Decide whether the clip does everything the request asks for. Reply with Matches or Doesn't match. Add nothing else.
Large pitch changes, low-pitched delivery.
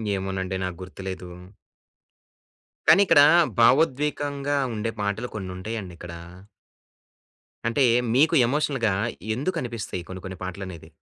Matches